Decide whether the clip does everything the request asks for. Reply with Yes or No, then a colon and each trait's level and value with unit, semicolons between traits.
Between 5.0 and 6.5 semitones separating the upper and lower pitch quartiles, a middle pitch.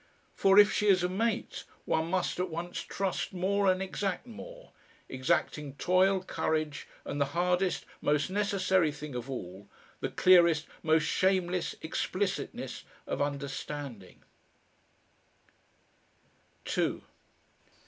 No: average, 4.2 semitones; medium, 180 Hz